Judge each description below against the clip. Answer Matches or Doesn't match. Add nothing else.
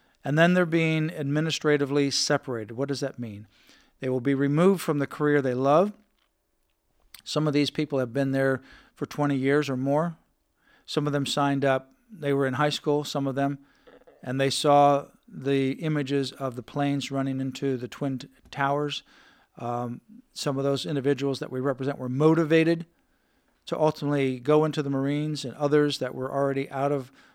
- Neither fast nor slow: Matches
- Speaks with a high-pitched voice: Doesn't match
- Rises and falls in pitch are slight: Matches